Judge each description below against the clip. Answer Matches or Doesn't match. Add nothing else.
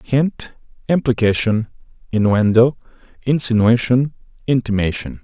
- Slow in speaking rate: Matches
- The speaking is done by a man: Matches